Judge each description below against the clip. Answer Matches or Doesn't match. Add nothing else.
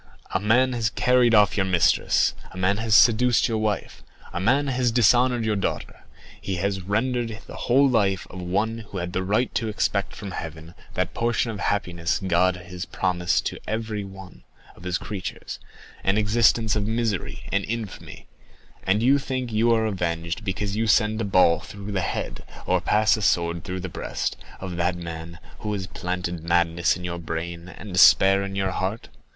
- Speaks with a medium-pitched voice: Doesn't match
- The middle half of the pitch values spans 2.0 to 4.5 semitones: Matches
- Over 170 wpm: Matches